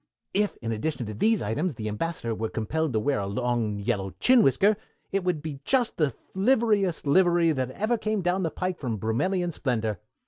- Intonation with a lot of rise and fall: Yes, wide, 9.0 semitones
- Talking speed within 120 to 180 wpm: No, average, 195 wpm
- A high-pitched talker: No, medium, 155 Hz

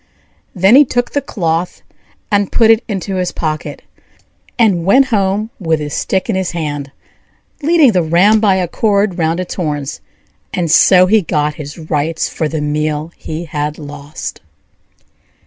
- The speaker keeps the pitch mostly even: No, average, 4.8 semitones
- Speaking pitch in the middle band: Yes, medium, 175 Hz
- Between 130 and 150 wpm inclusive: No, average, 160 wpm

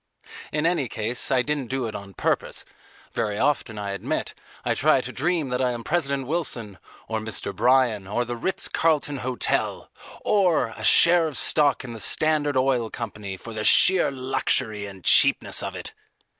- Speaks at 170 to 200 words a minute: Yes, average, 175 wpm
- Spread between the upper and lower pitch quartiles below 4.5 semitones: No, average, 5.0 semitones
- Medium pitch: No, low, 125 Hz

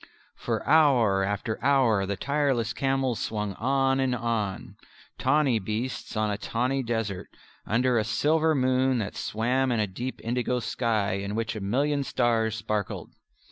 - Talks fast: No, average, 150 wpm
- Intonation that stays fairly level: No, average, 3.6 semitones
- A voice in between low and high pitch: No, low, 120 Hz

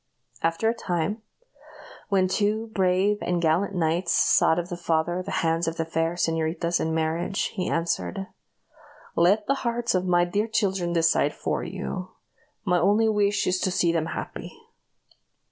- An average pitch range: Yes, average, 3.3 semitones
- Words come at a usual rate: Yes, average, 160 wpm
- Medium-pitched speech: Yes, medium, 175 Hz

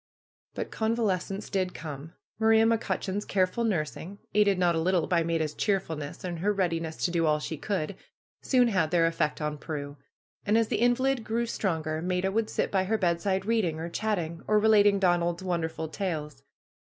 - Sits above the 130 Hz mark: Yes, medium, 185 Hz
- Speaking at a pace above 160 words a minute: Yes, average, 180 wpm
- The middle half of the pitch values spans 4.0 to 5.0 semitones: Yes, average, 4.3 semitones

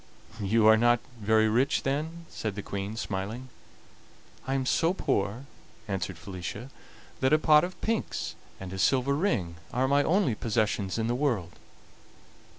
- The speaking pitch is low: Yes, low, 115 Hz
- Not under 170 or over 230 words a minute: No, average, 155 wpm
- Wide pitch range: Yes, wide, 5.7 semitones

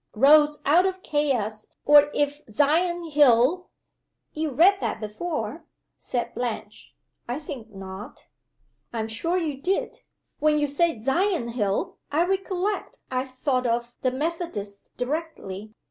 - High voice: Yes, very high, 290 Hz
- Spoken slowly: Yes, slow, 130 wpm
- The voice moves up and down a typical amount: No, wide, 5.9 semitones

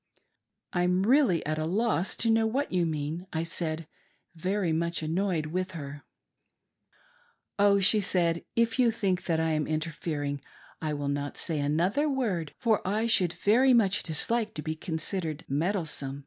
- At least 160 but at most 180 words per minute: Yes, average, 170 wpm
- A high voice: No, medium, 175 Hz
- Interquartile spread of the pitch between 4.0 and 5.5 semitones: Yes, average, 4.6 semitones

